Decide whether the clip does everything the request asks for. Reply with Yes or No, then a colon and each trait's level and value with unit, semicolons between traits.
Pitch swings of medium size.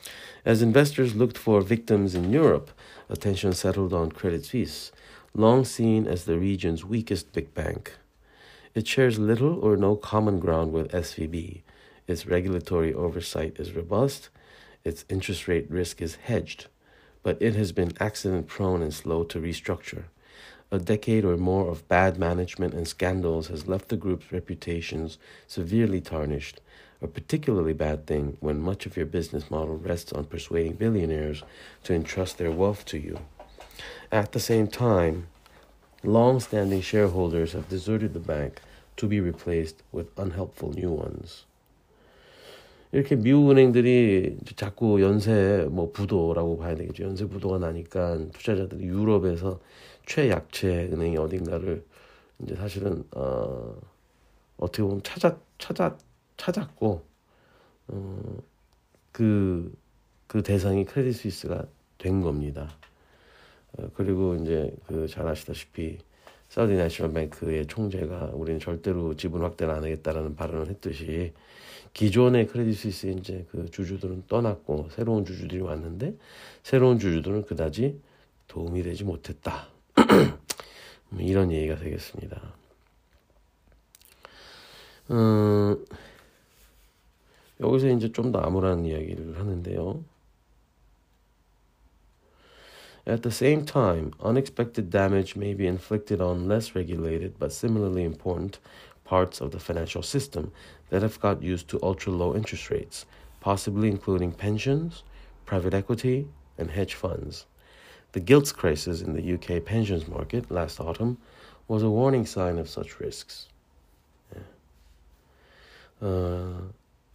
Yes: average, 4.5 semitones